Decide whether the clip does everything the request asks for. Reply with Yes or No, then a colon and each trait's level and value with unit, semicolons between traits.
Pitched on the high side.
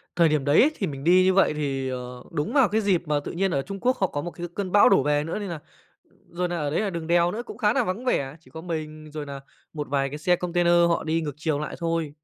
No: medium, 165 Hz